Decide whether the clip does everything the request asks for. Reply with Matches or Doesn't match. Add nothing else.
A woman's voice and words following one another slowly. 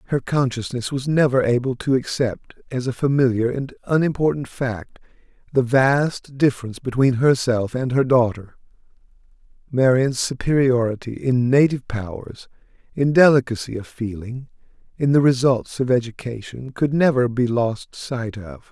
Doesn't match